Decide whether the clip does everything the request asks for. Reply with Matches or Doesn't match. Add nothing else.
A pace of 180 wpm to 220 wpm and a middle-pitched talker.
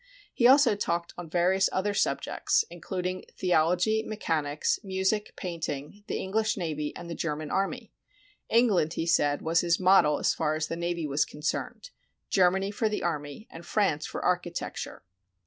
Doesn't match